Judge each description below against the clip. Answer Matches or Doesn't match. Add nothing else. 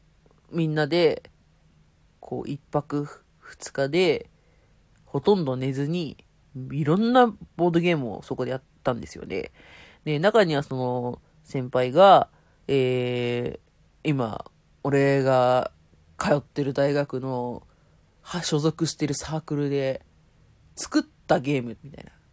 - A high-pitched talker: Doesn't match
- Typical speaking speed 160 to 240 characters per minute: Matches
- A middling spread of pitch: Matches